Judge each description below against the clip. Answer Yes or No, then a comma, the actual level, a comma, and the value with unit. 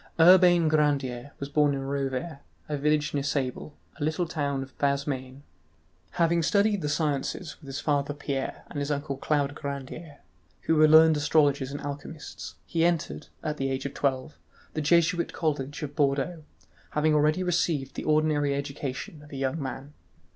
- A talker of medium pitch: Yes, medium, 145 Hz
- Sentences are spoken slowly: No, average, 170 wpm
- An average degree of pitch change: No, narrow, 2.2 semitones